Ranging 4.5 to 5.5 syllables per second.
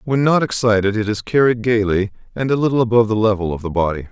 No: 6.7 syllables/s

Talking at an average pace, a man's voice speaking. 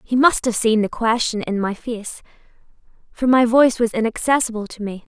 No: average, 185 wpm; female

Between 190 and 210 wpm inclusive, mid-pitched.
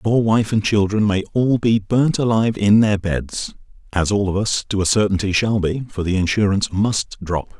No: average, 200 wpm; low, 105 Hz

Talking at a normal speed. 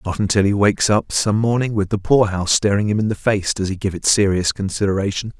No: fast, 235 wpm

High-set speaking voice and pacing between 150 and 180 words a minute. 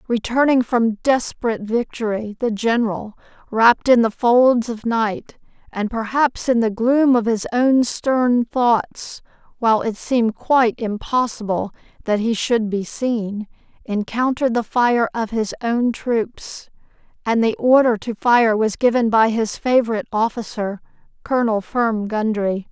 No: high, 230 Hz; average, 140 wpm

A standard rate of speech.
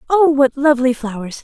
Yes: average, 165 wpm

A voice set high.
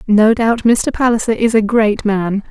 Yes: high, 220 Hz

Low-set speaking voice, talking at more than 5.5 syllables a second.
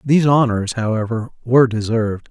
Yes: low, 120 Hz; 5.8 syllables/s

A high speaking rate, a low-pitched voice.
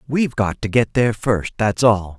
Yes: fast, 220 wpm; low, 115 Hz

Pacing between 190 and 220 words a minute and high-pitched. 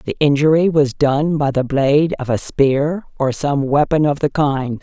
No: average, 200 wpm; medium, 145 Hz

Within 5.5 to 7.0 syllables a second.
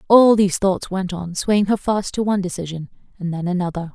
Yes: 5.7 syllables/s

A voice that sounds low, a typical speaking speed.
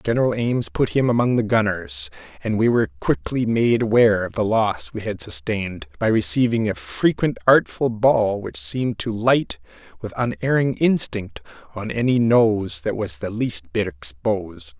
Yes: low, 115 Hz; average, 165 wpm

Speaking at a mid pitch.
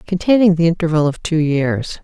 Yes: medium, 165 Hz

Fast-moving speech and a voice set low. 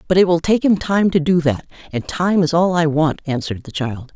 No: fast, 260 wpm; medium, 165 Hz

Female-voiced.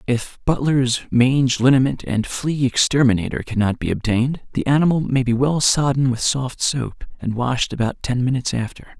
No: male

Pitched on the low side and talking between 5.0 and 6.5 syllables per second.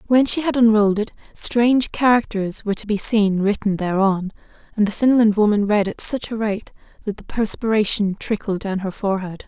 No: high, 210 Hz; 5.4 syllables/s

